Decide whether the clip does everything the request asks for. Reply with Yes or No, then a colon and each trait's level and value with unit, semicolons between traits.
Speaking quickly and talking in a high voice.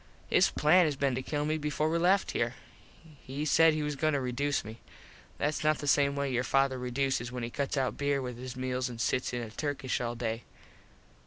No: fast, 225 wpm; low, 135 Hz